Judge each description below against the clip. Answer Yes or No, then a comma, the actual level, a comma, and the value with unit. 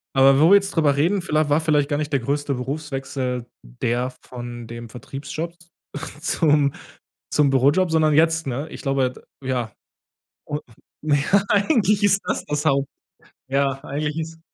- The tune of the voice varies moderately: Yes, average, 3.0 semitones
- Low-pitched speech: No, medium, 145 Hz